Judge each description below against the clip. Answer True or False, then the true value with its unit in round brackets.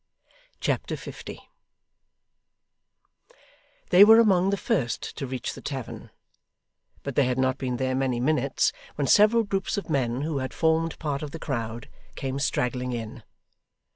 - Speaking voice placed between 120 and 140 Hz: True (135 Hz)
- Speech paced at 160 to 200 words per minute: False (145 wpm)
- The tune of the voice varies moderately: True (4.5 semitones)